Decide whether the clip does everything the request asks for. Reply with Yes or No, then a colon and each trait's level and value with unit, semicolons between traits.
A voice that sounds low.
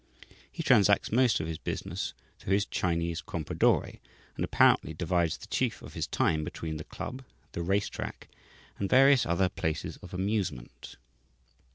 Yes: very low, 90 Hz